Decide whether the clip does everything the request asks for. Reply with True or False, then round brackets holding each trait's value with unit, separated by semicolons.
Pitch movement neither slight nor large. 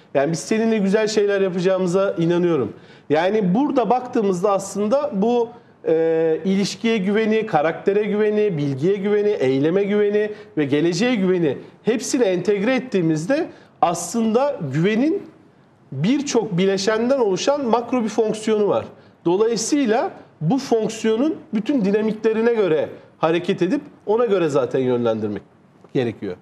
True (4.2 semitones)